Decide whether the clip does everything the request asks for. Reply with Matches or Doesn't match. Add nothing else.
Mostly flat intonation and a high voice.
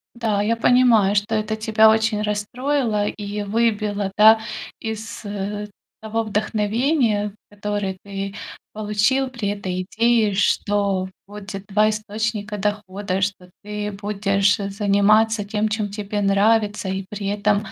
Matches